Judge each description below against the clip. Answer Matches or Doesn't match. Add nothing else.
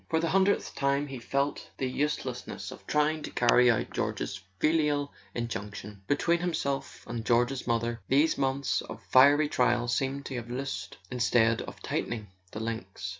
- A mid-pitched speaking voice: Doesn't match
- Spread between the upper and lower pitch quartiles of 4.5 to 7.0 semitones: Doesn't match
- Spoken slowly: Doesn't match